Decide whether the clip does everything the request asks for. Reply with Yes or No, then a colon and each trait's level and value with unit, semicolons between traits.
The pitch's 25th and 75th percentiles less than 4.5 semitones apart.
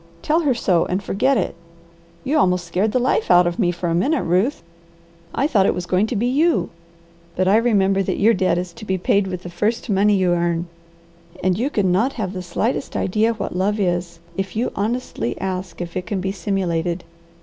Yes: average, 3.8 semitones